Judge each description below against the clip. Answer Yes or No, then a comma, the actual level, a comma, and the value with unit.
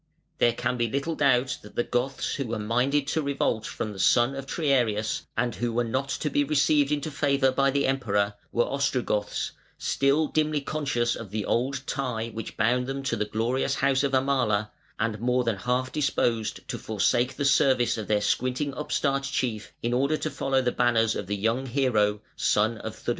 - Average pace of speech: Yes, average, 195 wpm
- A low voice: Yes, low, 125 Hz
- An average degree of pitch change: Yes, average, 3.4 semitones